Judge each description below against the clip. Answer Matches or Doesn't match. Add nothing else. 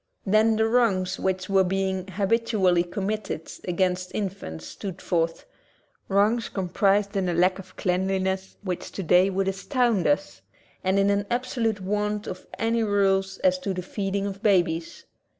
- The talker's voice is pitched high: Matches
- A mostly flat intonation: Matches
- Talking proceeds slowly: Doesn't match